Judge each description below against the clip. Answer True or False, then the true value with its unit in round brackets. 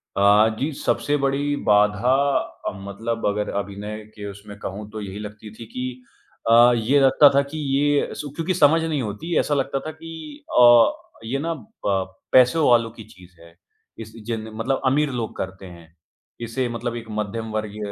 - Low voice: True (115 Hz)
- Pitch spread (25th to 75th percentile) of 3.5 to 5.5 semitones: True (5.1 semitones)